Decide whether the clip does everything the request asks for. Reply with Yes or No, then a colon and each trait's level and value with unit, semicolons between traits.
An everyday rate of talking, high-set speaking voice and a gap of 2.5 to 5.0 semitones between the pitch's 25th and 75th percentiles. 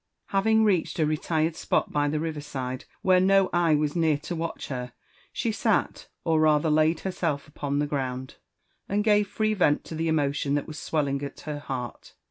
No: average, 190 wpm; medium, 155 Hz; average, 3.2 semitones